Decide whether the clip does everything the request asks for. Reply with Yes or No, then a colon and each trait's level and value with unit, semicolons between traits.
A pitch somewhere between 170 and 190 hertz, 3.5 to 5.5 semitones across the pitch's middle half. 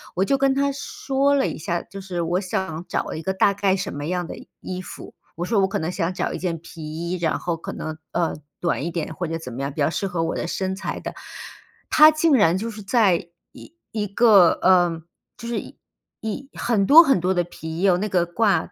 Yes: medium, 185 Hz; average, 3.9 semitones